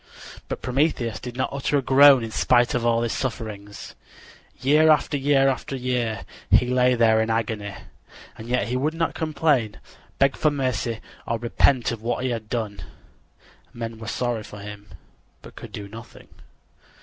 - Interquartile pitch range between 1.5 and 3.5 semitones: Yes, average, 3.2 semitones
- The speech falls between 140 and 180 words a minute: Yes, average, 160 wpm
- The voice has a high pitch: No, low, 120 Hz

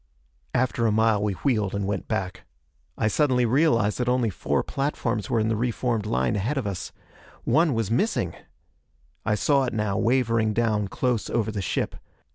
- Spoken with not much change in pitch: No, average, 3.0 semitones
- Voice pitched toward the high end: No, low, 115 Hz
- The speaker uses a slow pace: No, average, 180 wpm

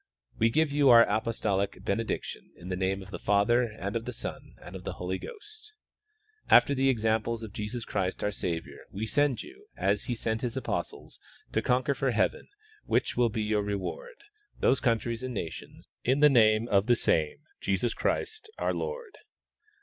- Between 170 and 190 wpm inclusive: Yes, average, 180 wpm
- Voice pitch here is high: No, low, 115 Hz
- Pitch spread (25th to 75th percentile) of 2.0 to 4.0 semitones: No, average, 4.4 semitones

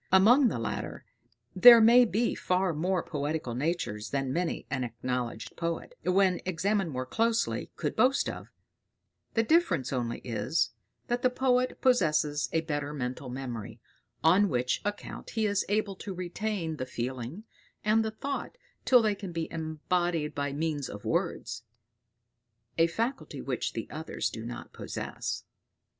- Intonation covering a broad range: Yes, wide, 7.4 semitones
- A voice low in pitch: No, medium, 170 Hz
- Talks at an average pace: Yes, average, 150 wpm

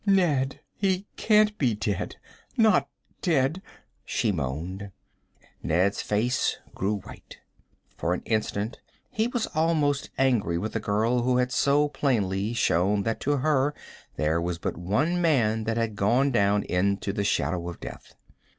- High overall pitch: No, low, 115 Hz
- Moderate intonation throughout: No, wide, 6.4 semitones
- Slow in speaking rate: No, average, 145 wpm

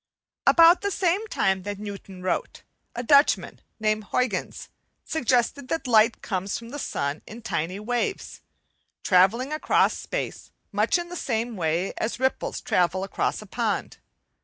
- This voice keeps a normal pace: Yes, average, 145 wpm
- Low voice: No, high, 225 Hz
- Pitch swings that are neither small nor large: No, wide, 6.5 semitones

